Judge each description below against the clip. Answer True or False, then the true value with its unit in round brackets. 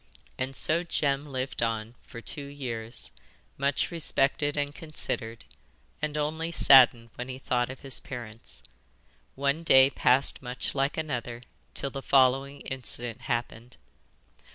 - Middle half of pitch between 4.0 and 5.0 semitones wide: False (2.8 semitones)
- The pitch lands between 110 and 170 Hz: True (135 Hz)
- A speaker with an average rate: False (130 wpm)